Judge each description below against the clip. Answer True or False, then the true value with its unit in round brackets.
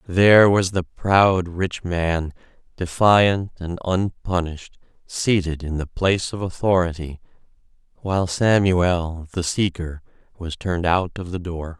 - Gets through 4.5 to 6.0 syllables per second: False (4.1 syllables/s)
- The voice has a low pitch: True (90 Hz)